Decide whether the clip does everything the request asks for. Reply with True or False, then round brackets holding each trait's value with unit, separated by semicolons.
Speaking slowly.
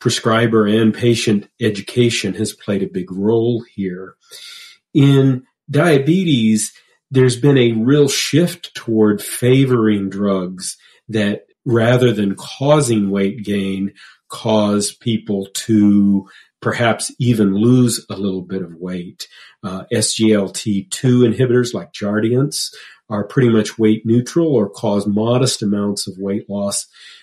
True (120 wpm)